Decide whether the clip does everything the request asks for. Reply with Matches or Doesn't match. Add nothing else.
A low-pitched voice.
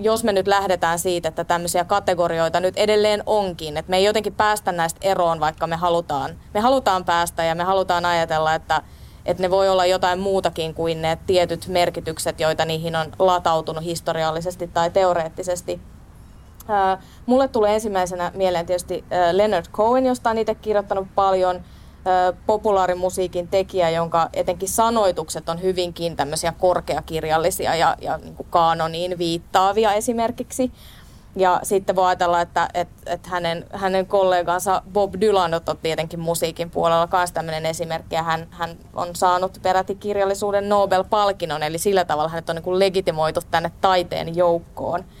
Doesn't match